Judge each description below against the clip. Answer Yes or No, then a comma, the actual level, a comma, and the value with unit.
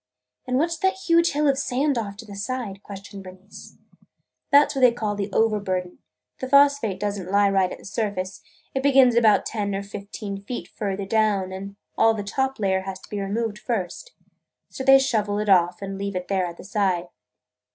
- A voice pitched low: No, high, 205 Hz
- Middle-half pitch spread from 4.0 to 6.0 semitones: Yes, average, 4.4 semitones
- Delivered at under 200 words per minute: No, fast, 205 wpm